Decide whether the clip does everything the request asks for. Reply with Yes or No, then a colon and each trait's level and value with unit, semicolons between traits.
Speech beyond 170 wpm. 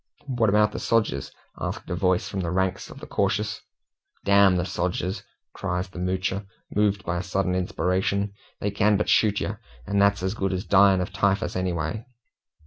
Yes: average, 180 wpm